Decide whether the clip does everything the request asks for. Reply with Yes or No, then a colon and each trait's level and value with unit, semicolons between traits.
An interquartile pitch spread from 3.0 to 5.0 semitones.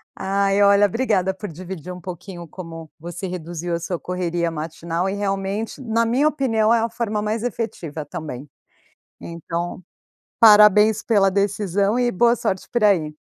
Yes: average, 3.9 semitones